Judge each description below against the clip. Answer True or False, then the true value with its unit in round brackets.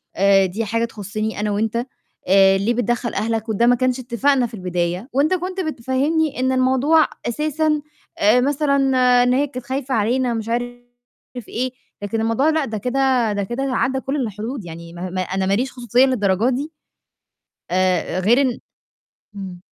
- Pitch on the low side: False (240 Hz)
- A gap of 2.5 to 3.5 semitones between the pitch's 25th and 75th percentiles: False (4.3 semitones)